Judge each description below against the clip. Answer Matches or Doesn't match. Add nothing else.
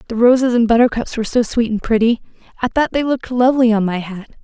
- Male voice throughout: Doesn't match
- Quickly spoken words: Matches